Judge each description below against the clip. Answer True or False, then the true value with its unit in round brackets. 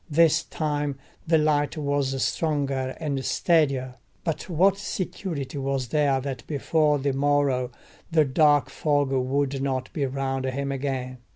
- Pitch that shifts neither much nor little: False (2.2 semitones)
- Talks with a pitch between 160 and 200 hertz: False (140 Hz)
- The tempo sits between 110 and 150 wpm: True (135 wpm)